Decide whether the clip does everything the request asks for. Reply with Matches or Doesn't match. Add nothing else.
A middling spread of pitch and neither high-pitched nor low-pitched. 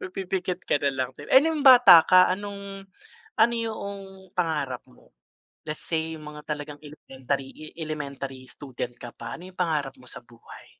Doesn't match